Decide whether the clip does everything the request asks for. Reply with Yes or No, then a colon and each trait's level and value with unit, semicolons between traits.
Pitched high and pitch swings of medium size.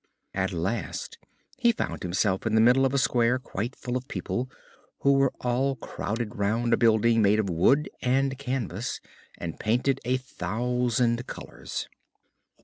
No: low, 120 Hz; average, 3.0 semitones